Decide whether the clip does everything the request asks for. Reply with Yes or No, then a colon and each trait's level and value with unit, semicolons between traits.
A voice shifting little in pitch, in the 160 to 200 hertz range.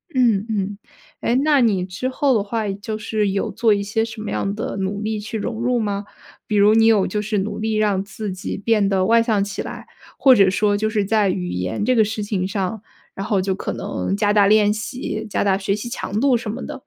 No: narrow, 2.1 semitones; high, 210 Hz